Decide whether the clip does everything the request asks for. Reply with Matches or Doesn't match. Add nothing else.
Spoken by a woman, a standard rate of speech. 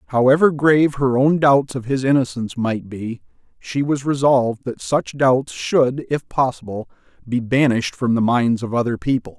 Doesn't match